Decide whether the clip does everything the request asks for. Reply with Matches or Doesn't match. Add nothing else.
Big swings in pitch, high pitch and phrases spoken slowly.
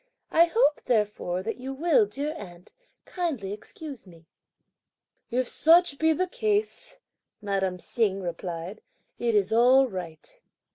Matches